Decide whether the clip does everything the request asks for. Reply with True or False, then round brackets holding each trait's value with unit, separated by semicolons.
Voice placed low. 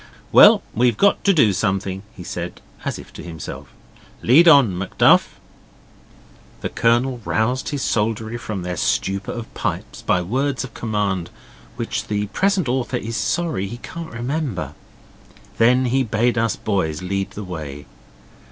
True (115 Hz)